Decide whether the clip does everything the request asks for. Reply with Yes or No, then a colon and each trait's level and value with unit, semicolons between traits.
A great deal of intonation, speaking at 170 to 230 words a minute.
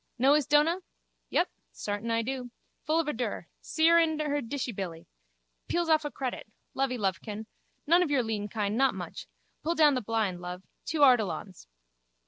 Yes: wide, 6.2 semitones; average, 175 wpm